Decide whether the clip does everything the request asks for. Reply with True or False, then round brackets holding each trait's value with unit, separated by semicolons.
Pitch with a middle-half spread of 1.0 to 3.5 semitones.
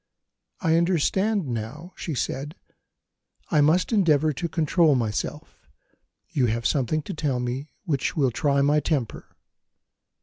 False (3.9 semitones)